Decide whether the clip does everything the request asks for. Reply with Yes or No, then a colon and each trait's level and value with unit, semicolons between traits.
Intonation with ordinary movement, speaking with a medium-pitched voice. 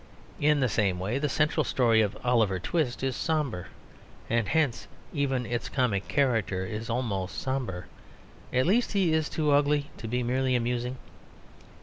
No: average, 4.4 semitones; low, 125 Hz